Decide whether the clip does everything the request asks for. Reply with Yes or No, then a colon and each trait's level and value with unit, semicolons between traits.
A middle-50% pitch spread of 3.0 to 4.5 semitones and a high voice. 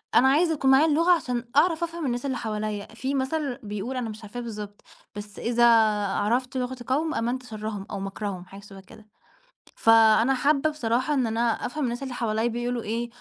Yes: average, 3.8 semitones; high, 240 Hz